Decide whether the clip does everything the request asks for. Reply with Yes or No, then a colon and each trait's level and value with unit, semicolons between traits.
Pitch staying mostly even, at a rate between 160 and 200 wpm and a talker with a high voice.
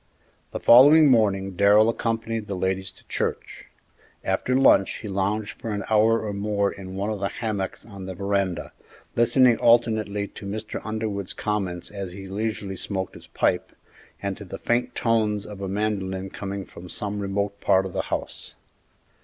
No: narrow, 2.1 semitones; average, 170 wpm; low, 100 Hz